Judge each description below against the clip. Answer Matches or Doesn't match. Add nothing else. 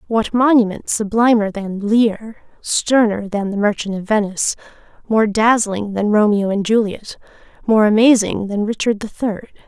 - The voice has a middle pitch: Doesn't match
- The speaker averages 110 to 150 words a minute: Matches